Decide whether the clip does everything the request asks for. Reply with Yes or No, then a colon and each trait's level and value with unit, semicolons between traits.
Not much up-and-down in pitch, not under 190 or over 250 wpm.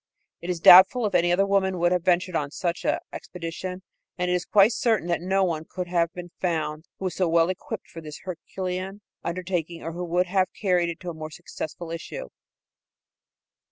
Yes: narrow, 1.9 semitones; fast, 205 wpm